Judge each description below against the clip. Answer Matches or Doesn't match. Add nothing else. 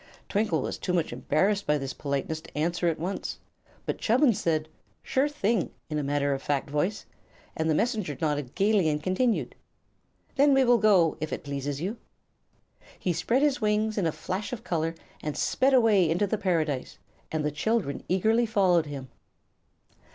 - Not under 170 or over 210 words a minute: Matches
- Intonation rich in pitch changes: Matches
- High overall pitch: Doesn't match